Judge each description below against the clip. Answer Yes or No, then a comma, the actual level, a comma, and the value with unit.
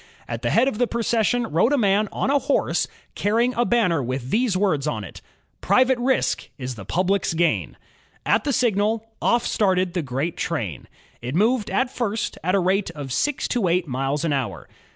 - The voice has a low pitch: No, high, 195 Hz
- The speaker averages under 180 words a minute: No, average, 195 wpm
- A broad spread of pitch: Yes, wide, 8.0 semitones